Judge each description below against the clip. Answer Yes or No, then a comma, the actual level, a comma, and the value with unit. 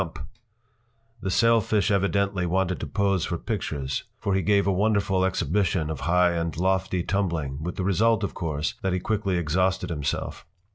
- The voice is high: No, very low, 95 Hz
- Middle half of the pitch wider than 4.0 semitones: No, average, 2.8 semitones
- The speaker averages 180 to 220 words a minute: No, average, 170 wpm